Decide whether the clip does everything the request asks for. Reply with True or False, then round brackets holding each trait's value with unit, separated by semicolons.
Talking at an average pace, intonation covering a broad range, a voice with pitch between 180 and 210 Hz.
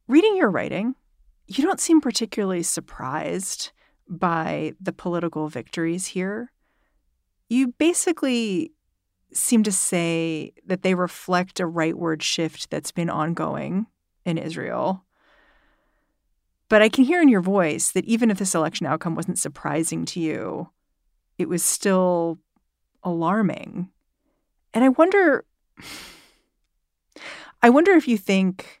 False (120 wpm; 6.5 semitones; 190 Hz)